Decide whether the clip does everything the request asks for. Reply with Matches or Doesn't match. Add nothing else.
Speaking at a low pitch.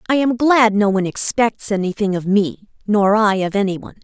Doesn't match